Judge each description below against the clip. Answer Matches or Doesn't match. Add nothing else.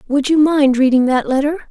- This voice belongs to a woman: Matches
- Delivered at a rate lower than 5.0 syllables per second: Doesn't match